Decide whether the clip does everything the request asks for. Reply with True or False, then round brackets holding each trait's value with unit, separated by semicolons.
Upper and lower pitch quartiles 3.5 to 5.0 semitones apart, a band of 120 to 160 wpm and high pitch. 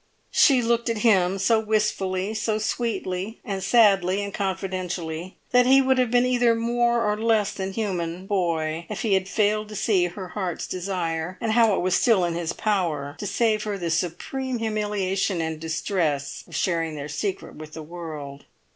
False (4.1 semitones; 180 wpm; 195 Hz)